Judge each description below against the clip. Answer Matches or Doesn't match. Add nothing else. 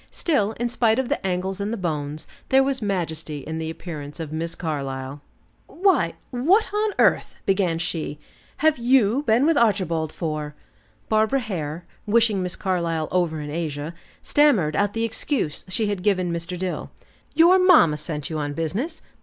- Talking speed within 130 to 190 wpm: Matches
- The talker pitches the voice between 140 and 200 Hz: Matches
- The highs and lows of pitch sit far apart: Matches